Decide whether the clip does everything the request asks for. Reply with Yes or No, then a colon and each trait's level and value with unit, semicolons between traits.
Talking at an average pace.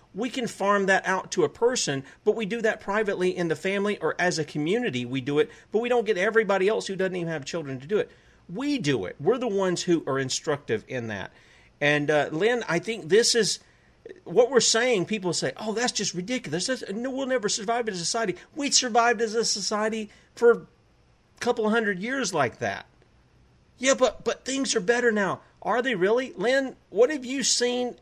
No: fast, 210 wpm